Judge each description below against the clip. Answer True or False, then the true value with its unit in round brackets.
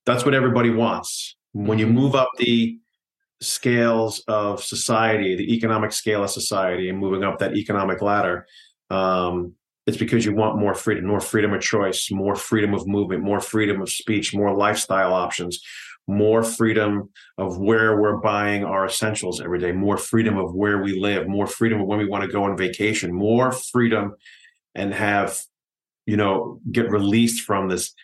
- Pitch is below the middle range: True (105 Hz)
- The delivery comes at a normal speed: True (175 wpm)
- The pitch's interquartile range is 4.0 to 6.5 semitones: False (2.5 semitones)